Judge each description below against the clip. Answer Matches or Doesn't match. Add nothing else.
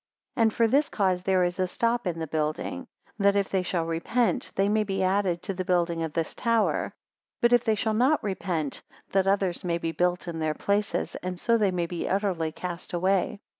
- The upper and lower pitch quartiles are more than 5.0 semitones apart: Doesn't match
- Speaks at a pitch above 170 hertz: Matches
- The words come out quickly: Matches